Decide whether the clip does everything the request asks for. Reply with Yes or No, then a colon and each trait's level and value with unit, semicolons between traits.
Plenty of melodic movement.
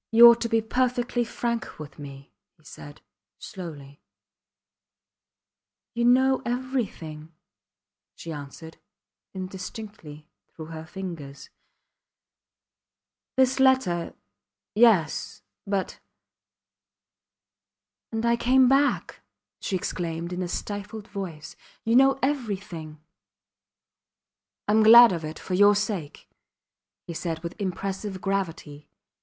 Yes: wide, 6.5 semitones